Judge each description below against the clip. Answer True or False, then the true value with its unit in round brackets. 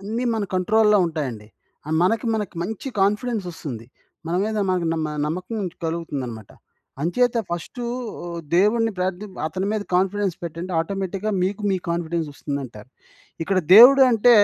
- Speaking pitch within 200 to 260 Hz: False (185 Hz)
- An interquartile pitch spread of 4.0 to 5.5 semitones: True (4.6 semitones)